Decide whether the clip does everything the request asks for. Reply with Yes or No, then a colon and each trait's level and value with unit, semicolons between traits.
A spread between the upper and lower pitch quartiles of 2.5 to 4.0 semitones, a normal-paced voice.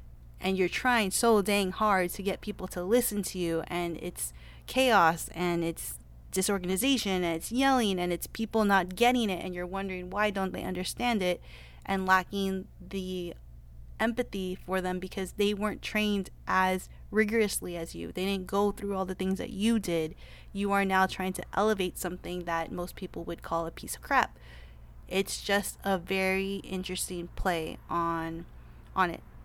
Yes: average, 2.8 semitones; average, 175 wpm